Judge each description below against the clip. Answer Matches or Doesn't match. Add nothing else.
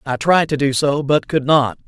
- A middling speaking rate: Doesn't match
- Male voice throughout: Matches